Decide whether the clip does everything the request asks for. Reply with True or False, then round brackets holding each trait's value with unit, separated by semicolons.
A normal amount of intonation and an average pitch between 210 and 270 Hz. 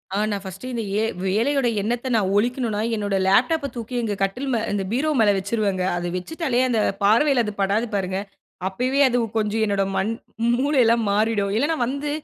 True (4.1 semitones; 225 Hz)